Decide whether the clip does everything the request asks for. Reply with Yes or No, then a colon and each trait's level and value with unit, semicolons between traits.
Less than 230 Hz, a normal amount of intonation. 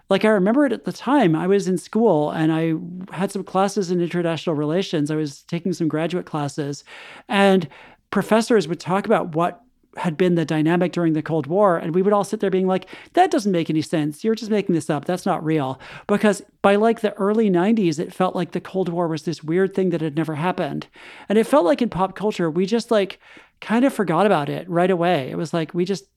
Yes: medium, 185 Hz; average, 3.8 semitones